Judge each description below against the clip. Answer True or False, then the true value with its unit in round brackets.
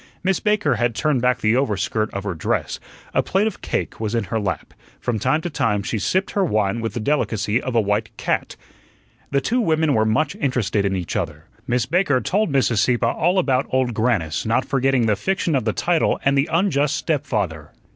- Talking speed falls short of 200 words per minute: False (205 wpm)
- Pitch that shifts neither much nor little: False (5.9 semitones)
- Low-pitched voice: True (125 Hz)